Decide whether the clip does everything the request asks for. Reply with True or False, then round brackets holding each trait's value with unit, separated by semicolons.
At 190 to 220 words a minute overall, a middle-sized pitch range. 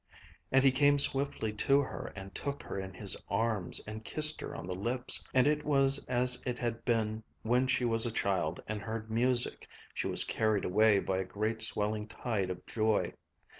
True (195 wpm; 3.5 semitones)